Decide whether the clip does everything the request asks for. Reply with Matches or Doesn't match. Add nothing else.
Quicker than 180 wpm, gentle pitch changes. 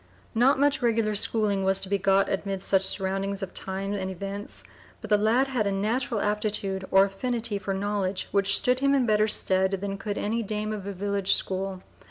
Matches